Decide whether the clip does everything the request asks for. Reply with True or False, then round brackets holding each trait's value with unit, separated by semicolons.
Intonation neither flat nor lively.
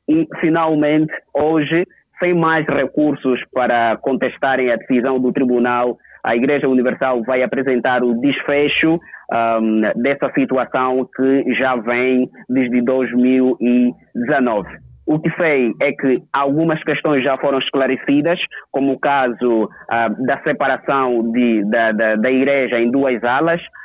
True (3.3 semitones)